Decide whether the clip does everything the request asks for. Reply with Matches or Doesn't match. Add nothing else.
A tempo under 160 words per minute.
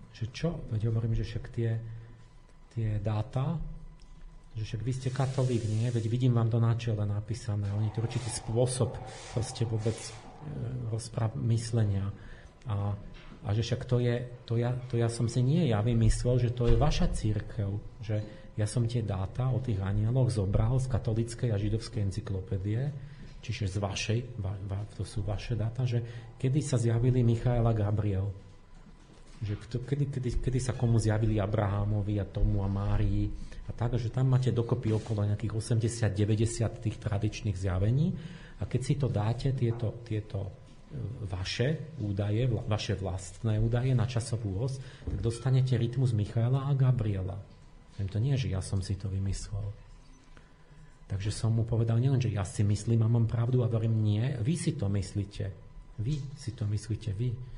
Doesn't match